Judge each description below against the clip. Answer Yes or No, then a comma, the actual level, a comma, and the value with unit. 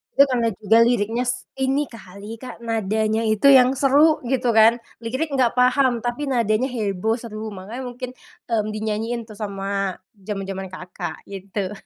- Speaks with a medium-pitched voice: No, high, 225 Hz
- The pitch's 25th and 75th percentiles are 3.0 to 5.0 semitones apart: Yes, average, 3.6 semitones